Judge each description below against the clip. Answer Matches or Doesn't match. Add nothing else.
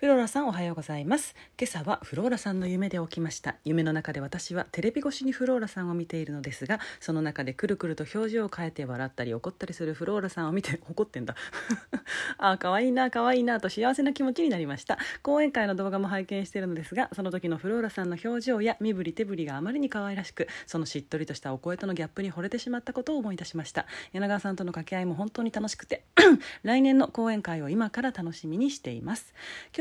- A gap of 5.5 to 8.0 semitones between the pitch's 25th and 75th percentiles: Matches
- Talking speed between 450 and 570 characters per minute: Matches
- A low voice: Doesn't match